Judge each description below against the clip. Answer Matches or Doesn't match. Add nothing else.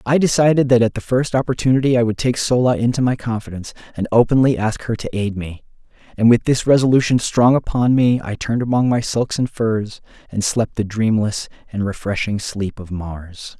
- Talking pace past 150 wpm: Matches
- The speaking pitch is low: Matches